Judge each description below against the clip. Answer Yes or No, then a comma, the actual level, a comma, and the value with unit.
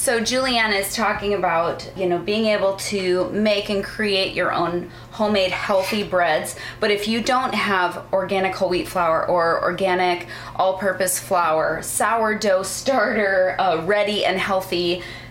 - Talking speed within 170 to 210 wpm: No, average, 145 wpm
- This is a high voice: Yes, high, 195 Hz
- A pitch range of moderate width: No, narrow, 2.3 semitones